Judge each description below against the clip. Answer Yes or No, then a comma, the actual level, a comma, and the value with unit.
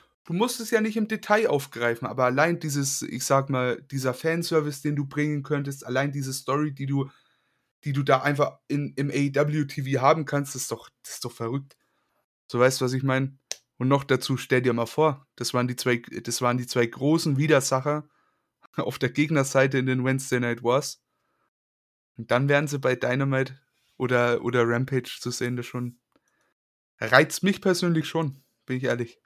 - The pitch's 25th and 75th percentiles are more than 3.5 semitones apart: No, average, 2.8 semitones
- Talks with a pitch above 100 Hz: Yes, low, 135 Hz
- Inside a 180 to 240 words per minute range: Yes, fast, 190 wpm